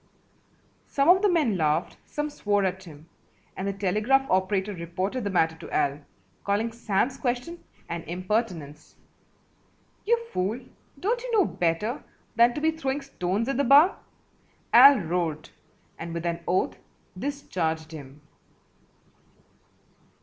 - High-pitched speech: Yes, high, 200 Hz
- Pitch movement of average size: No, wide, 8.1 semitones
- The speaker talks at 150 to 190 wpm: No, slow, 135 wpm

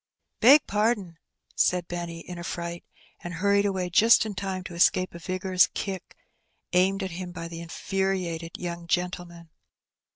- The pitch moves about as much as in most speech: No, narrow, 2.1 semitones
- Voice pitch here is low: No, medium, 180 Hz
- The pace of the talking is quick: No, average, 155 wpm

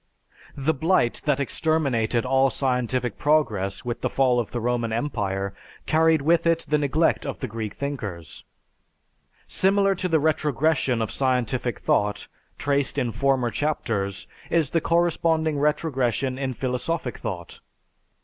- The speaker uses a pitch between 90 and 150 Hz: Yes, low, 135 Hz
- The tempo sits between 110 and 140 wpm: Yes, slow, 135 wpm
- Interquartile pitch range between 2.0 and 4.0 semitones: No, average, 4.6 semitones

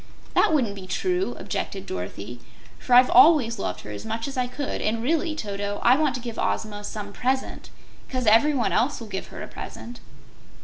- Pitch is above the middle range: Yes, high, 235 Hz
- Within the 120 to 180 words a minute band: No, average, 190 wpm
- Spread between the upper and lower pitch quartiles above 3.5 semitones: Yes, average, 4.7 semitones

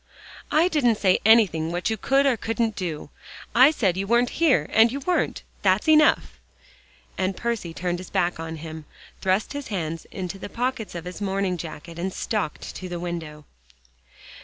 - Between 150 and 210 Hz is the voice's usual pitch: Yes, high, 190 Hz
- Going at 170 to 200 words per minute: Yes, average, 175 wpm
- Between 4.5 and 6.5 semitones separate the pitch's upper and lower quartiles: Yes, wide, 5.4 semitones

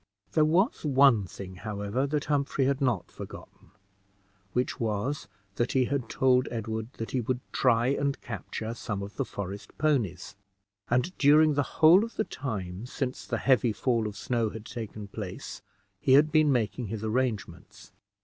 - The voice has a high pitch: No, low, 120 Hz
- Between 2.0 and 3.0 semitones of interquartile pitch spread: No, average, 4.6 semitones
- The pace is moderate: Yes, average, 165 wpm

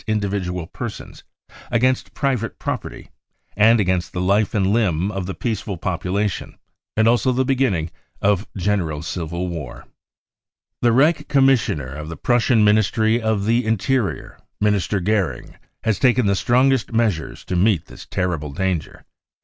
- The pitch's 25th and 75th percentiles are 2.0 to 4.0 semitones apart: No, average, 4.4 semitones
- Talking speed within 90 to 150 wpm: Yes, average, 140 wpm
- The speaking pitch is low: Yes, low, 105 Hz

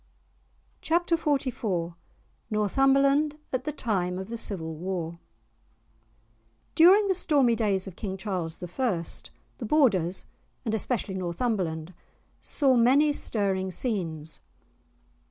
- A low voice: No, high, 210 Hz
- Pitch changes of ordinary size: No, wide, 7.0 semitones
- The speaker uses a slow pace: Yes, slow, 105 wpm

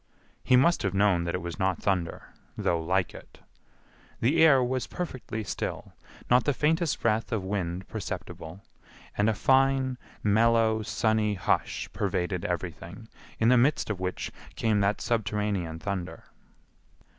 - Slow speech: No, average, 145 wpm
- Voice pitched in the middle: No, low, 105 Hz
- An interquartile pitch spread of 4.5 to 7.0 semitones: Yes, average, 4.8 semitones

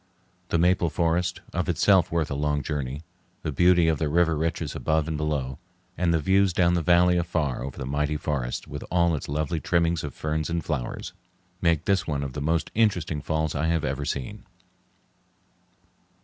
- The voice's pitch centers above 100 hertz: No, very low, 80 Hz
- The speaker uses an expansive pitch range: No, average, 2.8 semitones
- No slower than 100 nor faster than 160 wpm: No, average, 185 wpm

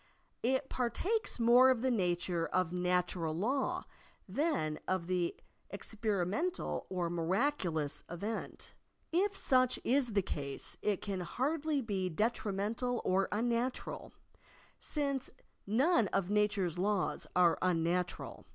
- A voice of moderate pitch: No, high, 205 Hz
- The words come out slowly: Yes, slow, 120 wpm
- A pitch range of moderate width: No, wide, 6.3 semitones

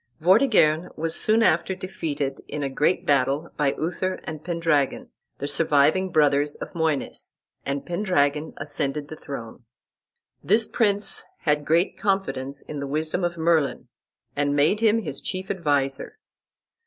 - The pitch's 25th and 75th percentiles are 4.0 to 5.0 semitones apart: Yes, average, 4.4 semitones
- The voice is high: No, medium, 155 Hz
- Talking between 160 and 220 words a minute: No, average, 140 wpm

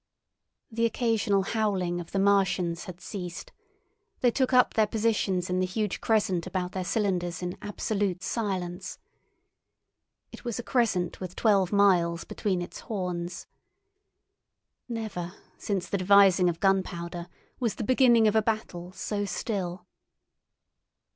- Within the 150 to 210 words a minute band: No, slow, 135 wpm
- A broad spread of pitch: No, average, 3.3 semitones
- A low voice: No, high, 195 Hz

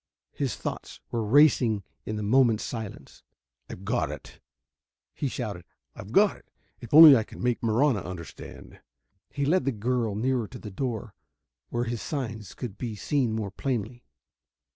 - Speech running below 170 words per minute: Yes, average, 160 wpm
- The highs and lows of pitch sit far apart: No, average, 3.6 semitones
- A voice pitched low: Yes, low, 115 Hz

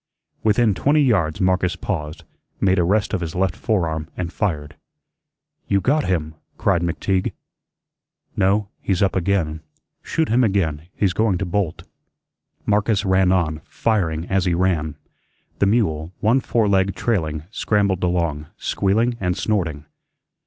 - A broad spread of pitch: No, average, 3.8 semitones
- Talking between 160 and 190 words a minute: No, average, 140 wpm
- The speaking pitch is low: Yes, very low, 95 Hz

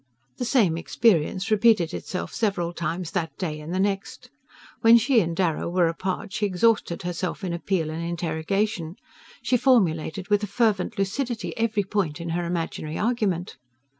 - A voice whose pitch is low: No, medium, 185 Hz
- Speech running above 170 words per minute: No, average, 160 wpm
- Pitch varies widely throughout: No, average, 4.1 semitones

